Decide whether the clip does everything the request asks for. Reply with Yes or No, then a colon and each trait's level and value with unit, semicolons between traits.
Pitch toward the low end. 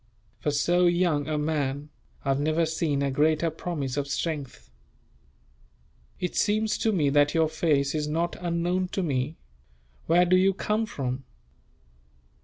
No: medium, 155 Hz